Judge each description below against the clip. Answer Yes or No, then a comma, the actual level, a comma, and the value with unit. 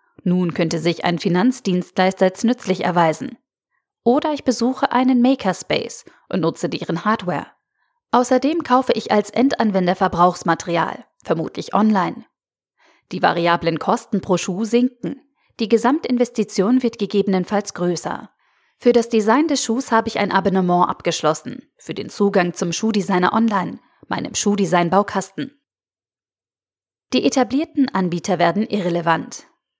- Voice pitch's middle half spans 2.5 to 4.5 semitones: No, wide, 5.5 semitones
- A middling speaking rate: No, slow, 120 wpm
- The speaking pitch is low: No, high, 205 Hz